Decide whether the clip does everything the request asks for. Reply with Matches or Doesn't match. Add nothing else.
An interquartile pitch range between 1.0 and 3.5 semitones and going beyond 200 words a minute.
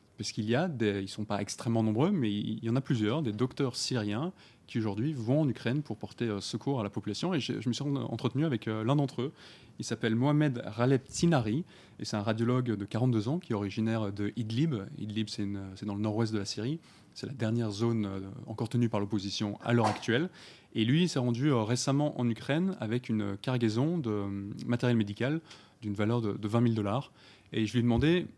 Doesn't match